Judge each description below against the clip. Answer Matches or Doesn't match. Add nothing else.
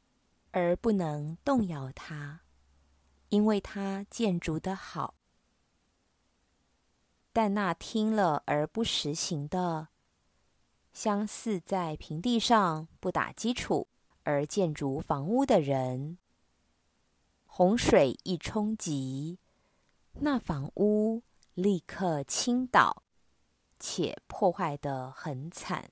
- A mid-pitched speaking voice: Matches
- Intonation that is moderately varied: Doesn't match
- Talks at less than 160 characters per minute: Matches